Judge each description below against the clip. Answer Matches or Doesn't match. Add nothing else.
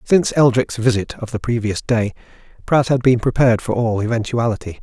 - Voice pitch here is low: Matches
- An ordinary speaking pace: Matches